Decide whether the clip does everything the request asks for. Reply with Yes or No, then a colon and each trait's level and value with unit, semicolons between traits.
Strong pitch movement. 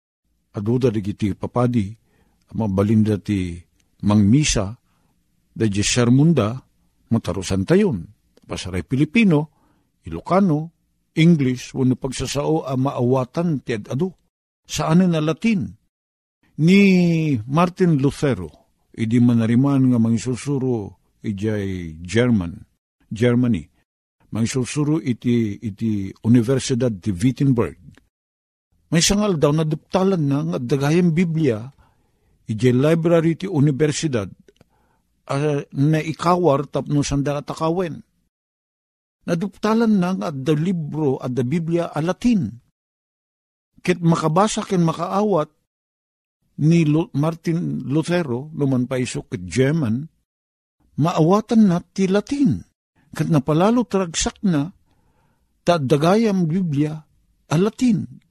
Yes: wide, 6.7 semitones